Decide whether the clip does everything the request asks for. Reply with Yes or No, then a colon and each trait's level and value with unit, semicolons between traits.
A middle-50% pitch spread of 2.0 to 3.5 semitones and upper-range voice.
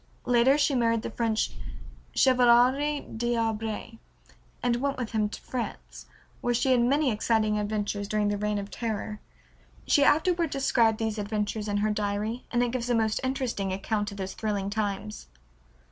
Yes: average, 2.7 semitones; high, 225 Hz